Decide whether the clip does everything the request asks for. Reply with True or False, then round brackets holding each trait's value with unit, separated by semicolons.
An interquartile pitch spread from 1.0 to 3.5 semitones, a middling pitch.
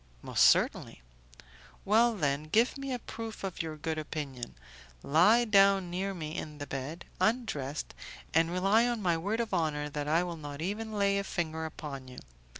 False (5.4 semitones; 170 Hz)